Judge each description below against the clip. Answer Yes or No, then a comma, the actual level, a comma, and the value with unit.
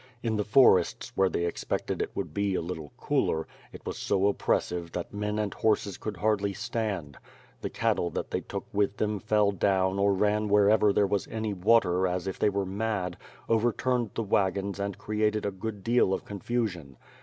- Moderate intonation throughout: No, narrow, 2.2 semitones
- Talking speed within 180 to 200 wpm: Yes, average, 190 wpm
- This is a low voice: Yes, low, 100 Hz